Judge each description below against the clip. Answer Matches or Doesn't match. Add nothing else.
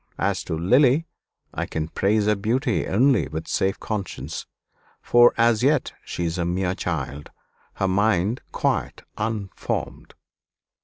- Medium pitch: Doesn't match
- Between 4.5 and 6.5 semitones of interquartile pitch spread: Matches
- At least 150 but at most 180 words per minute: Doesn't match